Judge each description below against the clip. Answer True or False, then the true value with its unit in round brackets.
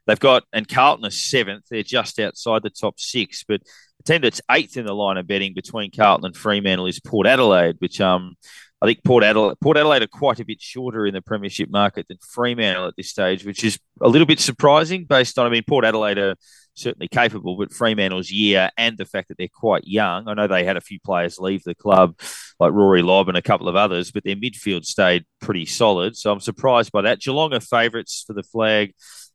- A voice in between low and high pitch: False (105 Hz)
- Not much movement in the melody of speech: False (3.5 semitones)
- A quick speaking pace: True (225 wpm)